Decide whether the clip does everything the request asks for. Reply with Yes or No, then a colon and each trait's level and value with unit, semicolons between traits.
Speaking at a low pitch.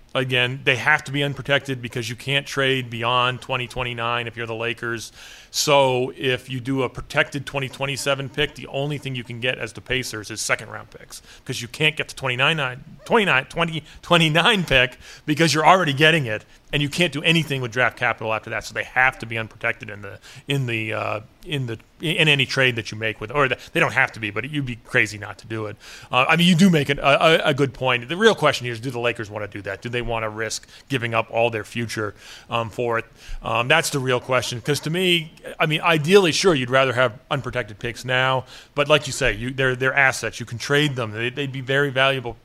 Yes: low, 130 Hz